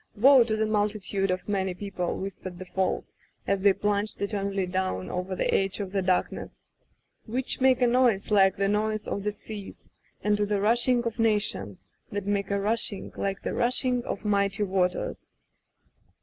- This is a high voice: Yes, high, 200 Hz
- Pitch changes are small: Yes, narrow, 2.1 semitones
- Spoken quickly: No, average, 185 wpm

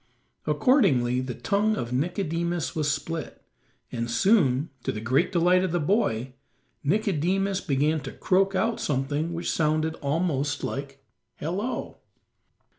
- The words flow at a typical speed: No, slow, 125 wpm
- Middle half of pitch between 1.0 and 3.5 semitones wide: No, wide, 5.4 semitones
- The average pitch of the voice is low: No, medium, 160 Hz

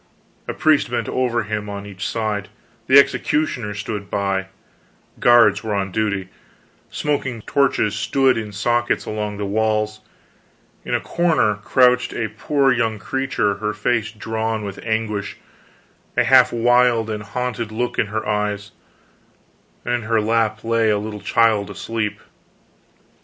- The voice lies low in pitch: Yes, low, 110 Hz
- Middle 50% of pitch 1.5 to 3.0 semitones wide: Yes, narrow, 2.6 semitones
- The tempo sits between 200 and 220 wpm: No, average, 140 wpm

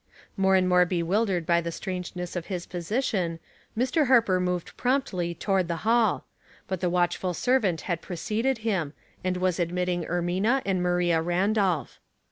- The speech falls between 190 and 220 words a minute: No, average, 160 wpm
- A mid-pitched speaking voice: Yes, medium, 180 Hz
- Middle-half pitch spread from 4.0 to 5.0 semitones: No, average, 2.9 semitones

